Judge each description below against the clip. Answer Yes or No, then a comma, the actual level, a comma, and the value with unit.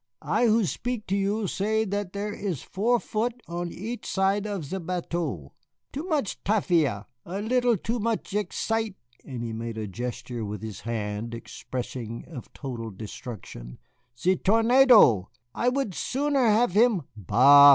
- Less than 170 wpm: Yes, average, 160 wpm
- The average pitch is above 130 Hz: Yes, high, 190 Hz